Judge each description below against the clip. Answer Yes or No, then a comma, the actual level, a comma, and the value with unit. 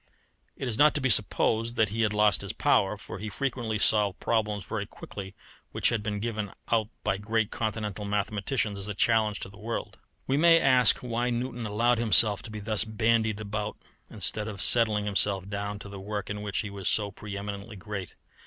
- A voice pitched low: Yes, low, 105 Hz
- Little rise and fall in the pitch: Yes, narrow, 2.0 semitones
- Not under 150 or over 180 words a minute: No, average, 200 wpm